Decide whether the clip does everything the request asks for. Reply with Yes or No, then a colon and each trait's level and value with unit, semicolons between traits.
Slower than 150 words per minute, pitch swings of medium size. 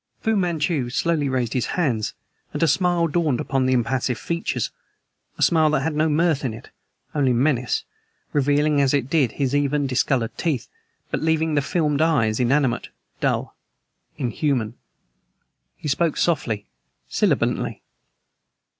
Yes: average, 140 wpm; average, 3.9 semitones